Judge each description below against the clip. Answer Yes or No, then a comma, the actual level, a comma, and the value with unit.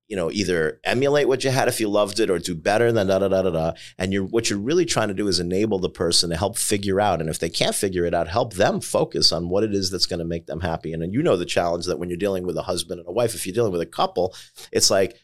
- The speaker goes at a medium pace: No, fast, 315 wpm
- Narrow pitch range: No, average, 4.5 semitones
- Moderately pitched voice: No, low, 100 Hz